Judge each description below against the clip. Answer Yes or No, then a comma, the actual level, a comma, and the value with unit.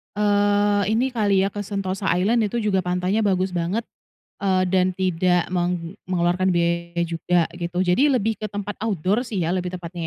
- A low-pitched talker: No, medium, 185 Hz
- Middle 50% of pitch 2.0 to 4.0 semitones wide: Yes, narrow, 2.6 semitones